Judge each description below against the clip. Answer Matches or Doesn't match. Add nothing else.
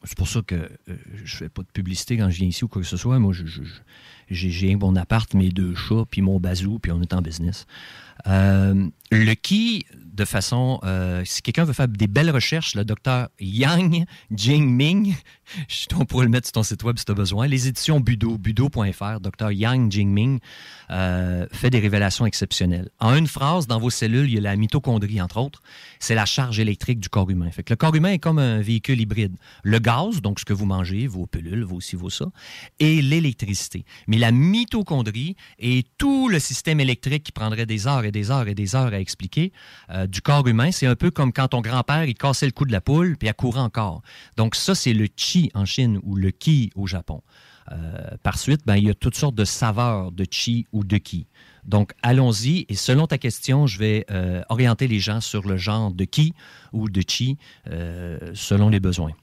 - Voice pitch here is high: Doesn't match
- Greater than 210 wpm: Matches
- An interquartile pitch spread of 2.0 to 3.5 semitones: Doesn't match